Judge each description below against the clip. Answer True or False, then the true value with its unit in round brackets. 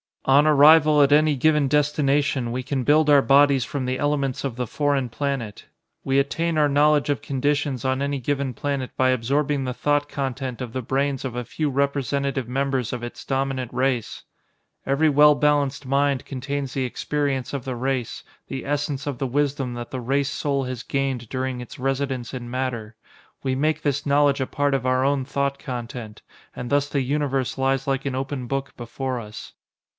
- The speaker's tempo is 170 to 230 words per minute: True (185 wpm)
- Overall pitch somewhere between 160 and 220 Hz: False (135 Hz)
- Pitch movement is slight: True (1.9 semitones)